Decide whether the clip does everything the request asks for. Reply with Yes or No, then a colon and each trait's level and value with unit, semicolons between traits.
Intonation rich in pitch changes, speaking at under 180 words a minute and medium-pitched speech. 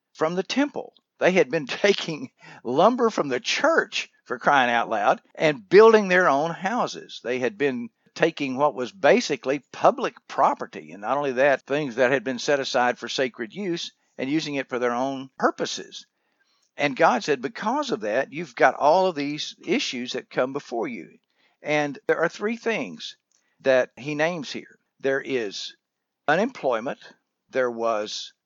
Yes: wide, 7.9 semitones; average, 165 wpm; medium, 150 Hz